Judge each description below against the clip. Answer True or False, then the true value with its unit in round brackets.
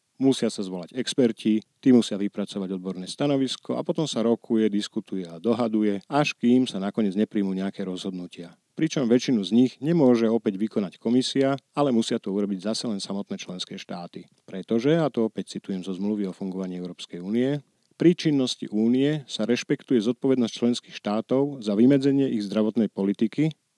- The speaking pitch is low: True (115 Hz)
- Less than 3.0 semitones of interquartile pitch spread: False (4.8 semitones)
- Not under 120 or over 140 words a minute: False (160 wpm)